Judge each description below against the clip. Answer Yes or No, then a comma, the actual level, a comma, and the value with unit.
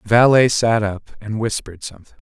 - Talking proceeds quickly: No, average, 185 wpm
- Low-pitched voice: Yes, low, 110 Hz